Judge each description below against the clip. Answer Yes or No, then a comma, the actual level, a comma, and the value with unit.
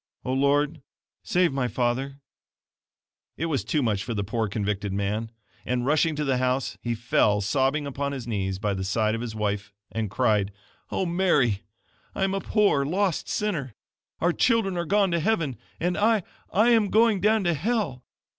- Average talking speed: Yes, average, 180 wpm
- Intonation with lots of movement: Yes, wide, 8.1 semitones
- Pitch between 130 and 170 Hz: Yes, low, 135 Hz